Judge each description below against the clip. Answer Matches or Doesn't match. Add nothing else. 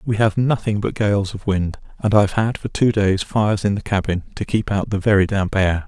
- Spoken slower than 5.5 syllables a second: Matches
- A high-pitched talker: Doesn't match